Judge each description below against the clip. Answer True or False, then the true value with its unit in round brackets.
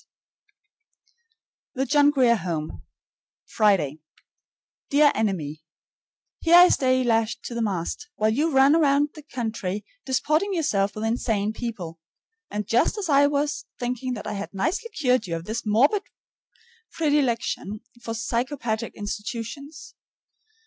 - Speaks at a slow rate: True (130 wpm)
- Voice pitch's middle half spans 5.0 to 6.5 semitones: True (5.4 semitones)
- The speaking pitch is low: False (235 Hz)